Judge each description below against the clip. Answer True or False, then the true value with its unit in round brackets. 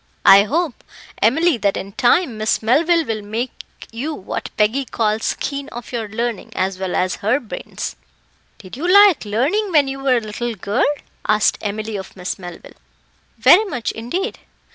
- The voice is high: True (230 Hz)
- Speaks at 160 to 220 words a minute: True (165 wpm)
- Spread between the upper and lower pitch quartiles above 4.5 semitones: True (5.0 semitones)